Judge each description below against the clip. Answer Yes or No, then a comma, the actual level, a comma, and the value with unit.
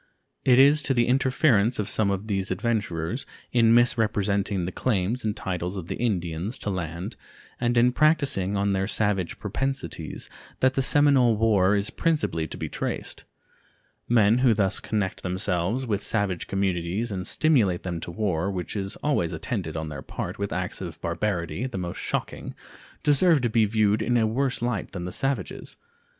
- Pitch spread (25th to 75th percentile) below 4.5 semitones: No, average, 4.8 semitones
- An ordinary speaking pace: Yes, average, 170 wpm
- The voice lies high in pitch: No, low, 105 Hz